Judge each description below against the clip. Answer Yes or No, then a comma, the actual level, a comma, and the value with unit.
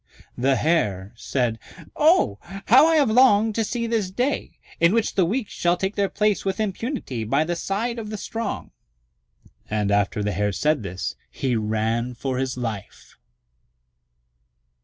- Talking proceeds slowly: No, average, 160 wpm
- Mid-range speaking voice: Yes, medium, 170 Hz